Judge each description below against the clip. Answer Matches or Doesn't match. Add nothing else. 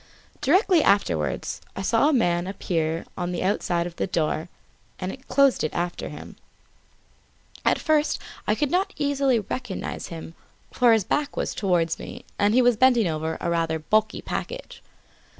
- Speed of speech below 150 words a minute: Doesn't match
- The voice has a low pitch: Doesn't match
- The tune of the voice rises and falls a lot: Matches